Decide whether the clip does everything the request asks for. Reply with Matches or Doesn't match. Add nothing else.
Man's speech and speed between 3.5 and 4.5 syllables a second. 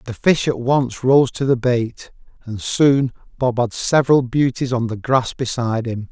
Matches